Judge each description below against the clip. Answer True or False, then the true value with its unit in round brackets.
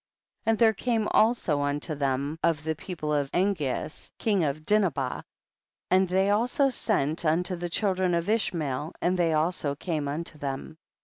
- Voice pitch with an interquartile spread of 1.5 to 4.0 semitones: False (4.7 semitones)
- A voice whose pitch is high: False (170 Hz)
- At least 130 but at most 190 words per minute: True (170 wpm)